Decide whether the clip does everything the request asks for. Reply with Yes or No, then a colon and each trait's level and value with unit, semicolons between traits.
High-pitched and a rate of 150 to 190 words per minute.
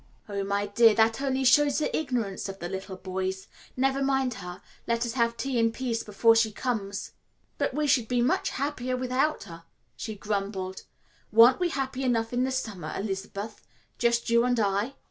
Yes: high, 230 Hz; average, 185 wpm